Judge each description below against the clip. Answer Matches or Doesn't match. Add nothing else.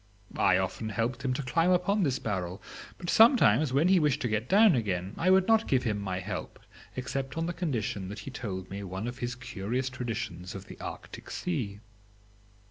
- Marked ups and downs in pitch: Matches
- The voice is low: Matches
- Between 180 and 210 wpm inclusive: Matches